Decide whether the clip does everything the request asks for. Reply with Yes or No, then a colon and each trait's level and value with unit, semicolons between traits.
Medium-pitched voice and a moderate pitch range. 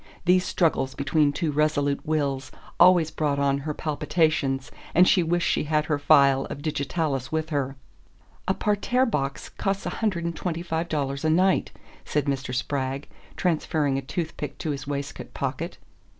Yes: medium, 150 Hz; average, 3.2 semitones